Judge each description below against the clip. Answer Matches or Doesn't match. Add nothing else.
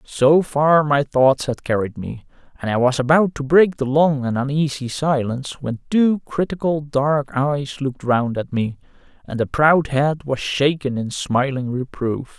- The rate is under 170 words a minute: Doesn't match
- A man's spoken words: Matches